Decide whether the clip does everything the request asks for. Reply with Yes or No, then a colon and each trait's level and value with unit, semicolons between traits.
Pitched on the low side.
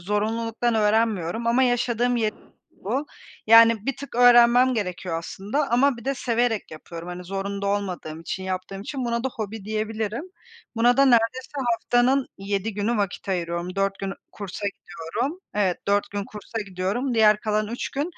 No: high, 215 Hz